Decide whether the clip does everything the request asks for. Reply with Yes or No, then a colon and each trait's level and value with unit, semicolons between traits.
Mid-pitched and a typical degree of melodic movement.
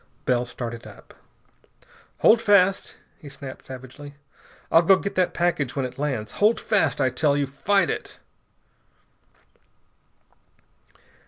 No: medium, 145 Hz; wide, 6.2 semitones